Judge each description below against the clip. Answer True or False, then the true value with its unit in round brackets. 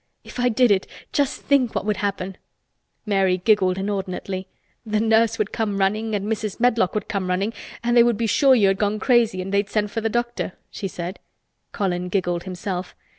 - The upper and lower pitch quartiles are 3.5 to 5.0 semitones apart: False (3.0 semitones)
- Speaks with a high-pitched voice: True (205 Hz)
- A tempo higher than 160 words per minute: True (195 wpm)